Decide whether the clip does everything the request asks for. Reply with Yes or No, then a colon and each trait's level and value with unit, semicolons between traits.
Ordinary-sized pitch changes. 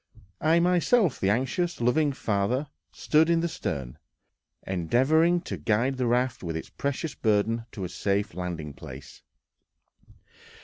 No: wide, 8.5 semitones